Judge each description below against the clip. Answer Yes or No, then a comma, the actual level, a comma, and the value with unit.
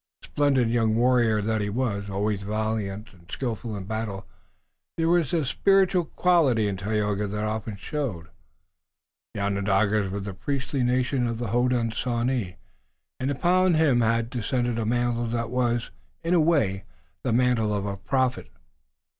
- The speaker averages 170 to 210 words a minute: No, average, 150 wpm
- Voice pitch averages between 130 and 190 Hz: No, low, 115 Hz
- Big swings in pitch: No, average, 3.7 semitones